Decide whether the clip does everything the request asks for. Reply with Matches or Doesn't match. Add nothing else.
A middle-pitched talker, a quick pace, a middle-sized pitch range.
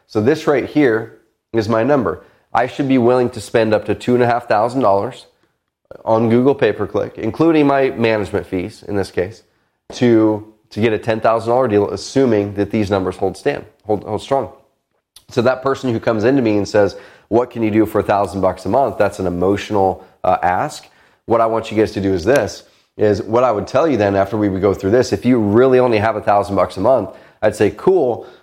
Doesn't match